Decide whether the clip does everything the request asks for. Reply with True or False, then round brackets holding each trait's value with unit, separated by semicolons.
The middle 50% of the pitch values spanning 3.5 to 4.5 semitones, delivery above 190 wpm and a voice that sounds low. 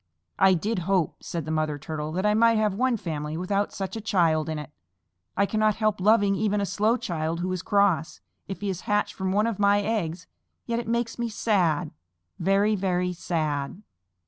False (4.2 semitones; 200 wpm; 195 Hz)